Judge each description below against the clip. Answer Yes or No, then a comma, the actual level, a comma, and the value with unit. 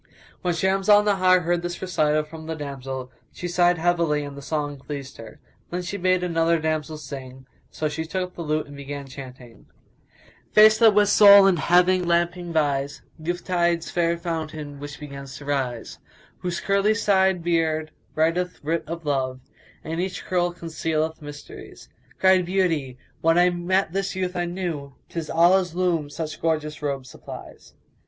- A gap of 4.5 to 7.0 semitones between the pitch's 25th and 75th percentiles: No, average, 3.5 semitones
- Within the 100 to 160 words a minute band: No, average, 175 wpm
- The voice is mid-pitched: Yes, medium, 165 Hz